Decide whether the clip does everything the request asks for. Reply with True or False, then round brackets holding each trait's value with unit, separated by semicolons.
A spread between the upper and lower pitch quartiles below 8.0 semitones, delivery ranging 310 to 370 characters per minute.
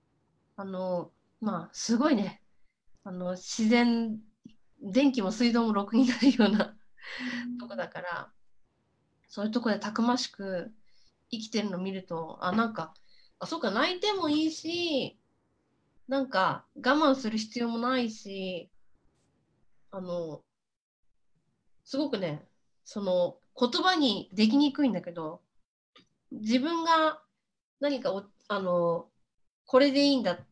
False (5.3 semitones; 230 characters per minute)